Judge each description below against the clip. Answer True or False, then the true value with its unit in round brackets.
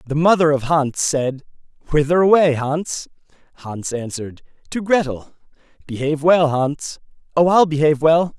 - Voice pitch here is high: False (150 Hz)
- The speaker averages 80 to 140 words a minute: True (135 wpm)